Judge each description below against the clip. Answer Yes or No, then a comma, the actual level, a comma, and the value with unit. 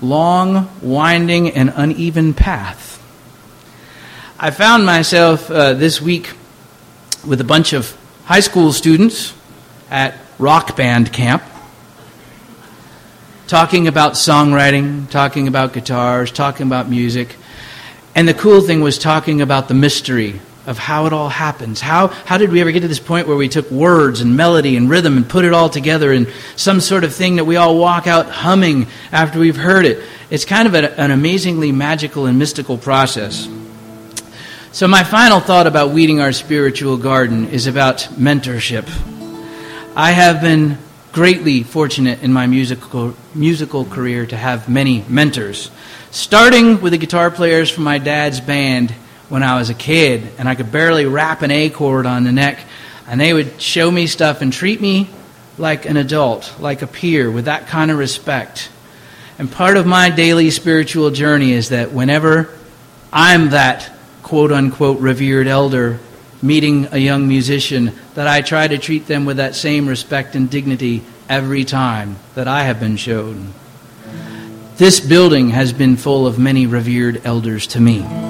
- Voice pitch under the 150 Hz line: Yes, medium, 140 Hz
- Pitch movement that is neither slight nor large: Yes, average, 4.2 semitones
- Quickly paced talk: No, average, 165 wpm